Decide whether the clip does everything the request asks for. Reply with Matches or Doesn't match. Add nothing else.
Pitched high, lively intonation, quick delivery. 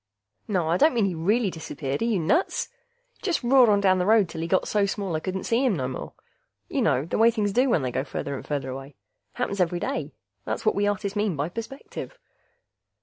Matches